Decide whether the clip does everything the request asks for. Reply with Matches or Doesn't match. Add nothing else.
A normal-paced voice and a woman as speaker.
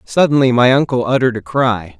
Doesn't match